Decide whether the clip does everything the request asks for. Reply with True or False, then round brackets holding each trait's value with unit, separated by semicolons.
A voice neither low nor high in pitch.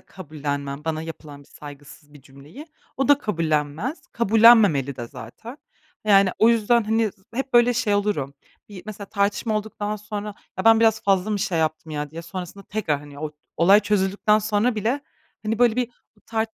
False (200 Hz)